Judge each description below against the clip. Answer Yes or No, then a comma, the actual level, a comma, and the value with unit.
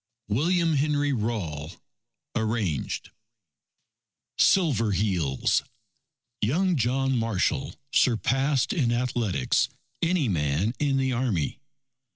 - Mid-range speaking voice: No, low, 120 Hz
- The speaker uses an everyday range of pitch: No, wide, 5.8 semitones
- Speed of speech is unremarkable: No, slow, 85 wpm